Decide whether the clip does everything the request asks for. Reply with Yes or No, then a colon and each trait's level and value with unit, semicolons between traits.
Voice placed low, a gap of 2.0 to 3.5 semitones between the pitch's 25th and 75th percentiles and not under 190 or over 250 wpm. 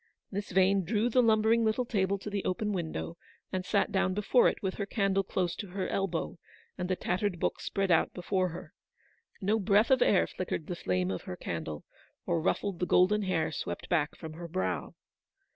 No: high, 190 Hz; average, 2.9 semitones; average, 195 wpm